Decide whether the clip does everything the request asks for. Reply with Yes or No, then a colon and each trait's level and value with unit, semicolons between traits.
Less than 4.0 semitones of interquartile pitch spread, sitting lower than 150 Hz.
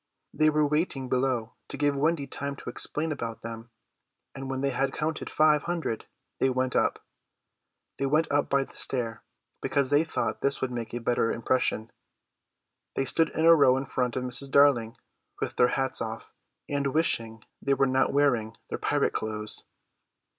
Yes: average, 3.1 semitones; low, 135 Hz